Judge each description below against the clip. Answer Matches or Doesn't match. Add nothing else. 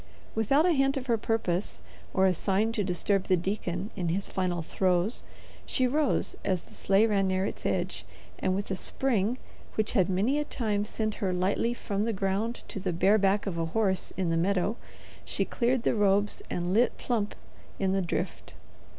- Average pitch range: Matches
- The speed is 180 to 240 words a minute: Matches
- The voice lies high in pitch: Matches